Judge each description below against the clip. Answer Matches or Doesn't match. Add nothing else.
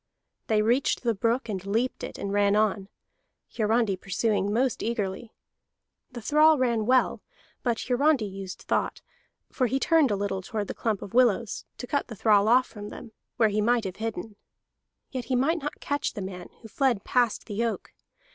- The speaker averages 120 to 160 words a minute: Doesn't match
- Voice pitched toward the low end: Doesn't match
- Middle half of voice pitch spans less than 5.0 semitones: Matches